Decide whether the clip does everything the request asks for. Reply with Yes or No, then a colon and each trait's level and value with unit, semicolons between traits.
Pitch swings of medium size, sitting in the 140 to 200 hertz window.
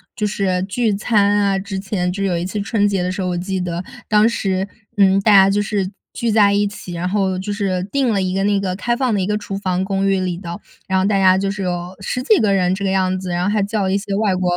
No: narrow, 1.8 semitones; high, 195 Hz